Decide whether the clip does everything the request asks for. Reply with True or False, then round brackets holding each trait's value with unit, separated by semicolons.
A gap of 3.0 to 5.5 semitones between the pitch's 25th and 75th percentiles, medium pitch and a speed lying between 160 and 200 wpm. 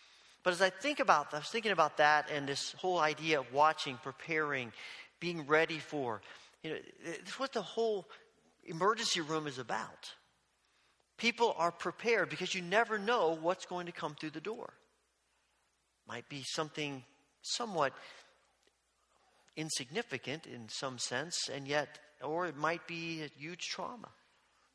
False (3.6 semitones; 160 Hz; 145 wpm)